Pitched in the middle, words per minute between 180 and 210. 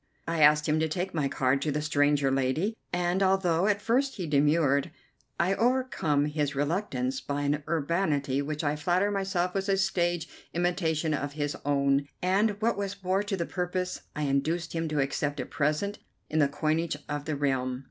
Yes: medium, 155 Hz; average, 185 wpm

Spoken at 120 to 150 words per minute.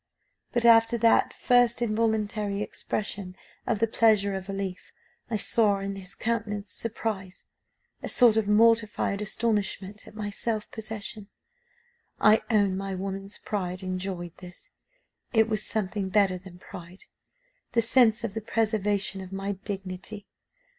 Yes: slow, 135 wpm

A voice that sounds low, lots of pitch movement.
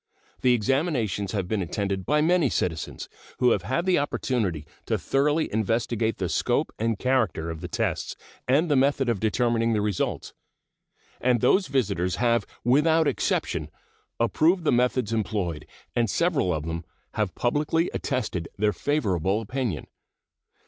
Yes: low, 115 Hz; wide, 5.7 semitones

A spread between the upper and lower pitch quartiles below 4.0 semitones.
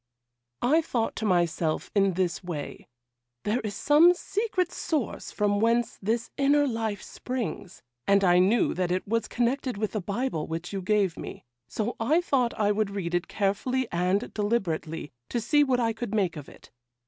No: average, 4.9 semitones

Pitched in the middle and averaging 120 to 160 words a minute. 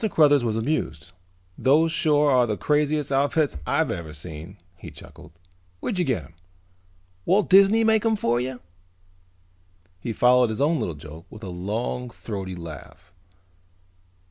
No: low, 125 Hz; average, 145 wpm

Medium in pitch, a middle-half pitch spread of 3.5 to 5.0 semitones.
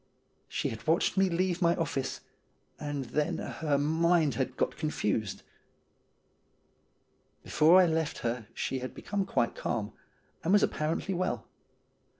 Yes: medium, 155 Hz; average, 4.6 semitones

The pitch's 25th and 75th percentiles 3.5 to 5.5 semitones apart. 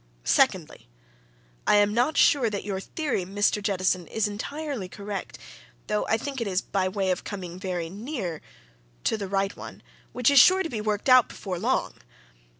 Yes: average, 4.2 semitones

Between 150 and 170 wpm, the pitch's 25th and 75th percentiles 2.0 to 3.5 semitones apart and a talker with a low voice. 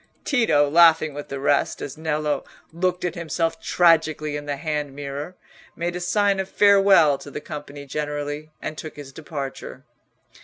No: average, 160 wpm; average, 2.9 semitones; medium, 155 Hz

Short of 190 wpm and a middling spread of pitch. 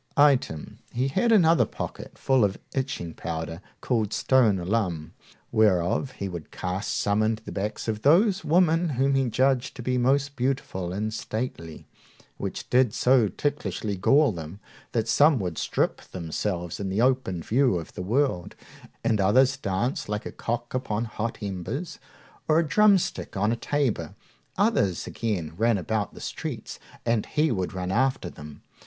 No: average, 160 wpm; wide, 6.1 semitones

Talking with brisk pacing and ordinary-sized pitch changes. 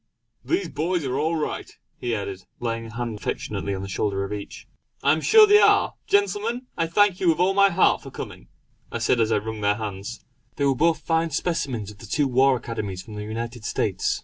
No: fast, 220 wpm; wide, 7.9 semitones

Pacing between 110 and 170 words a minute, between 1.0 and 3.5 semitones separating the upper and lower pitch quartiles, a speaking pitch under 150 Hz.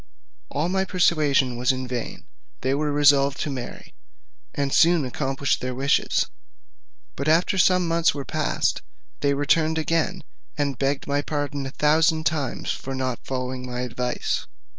Yes: average, 150 wpm; average, 3.2 semitones; medium, 140 Hz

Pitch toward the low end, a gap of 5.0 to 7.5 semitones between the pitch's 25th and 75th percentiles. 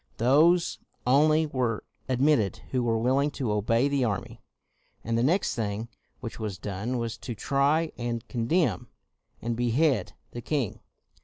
No: low, 120 Hz; average, 3.8 semitones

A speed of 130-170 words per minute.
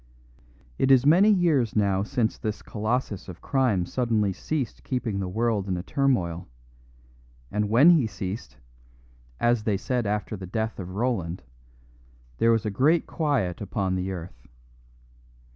Yes: average, 145 wpm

